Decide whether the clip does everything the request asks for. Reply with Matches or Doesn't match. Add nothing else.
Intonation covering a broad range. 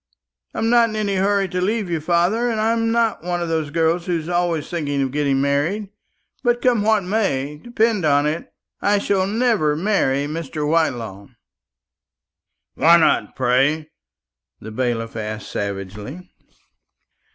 Matches